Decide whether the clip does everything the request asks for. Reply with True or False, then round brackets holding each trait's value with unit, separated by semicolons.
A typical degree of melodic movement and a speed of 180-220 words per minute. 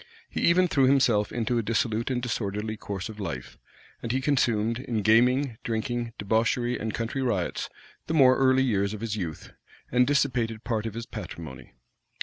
False (3.1 semitones; 170 wpm)